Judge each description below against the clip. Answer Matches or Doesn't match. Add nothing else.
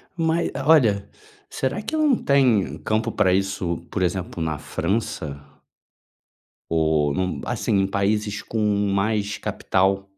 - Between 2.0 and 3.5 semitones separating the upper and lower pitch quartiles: Doesn't match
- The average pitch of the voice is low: Matches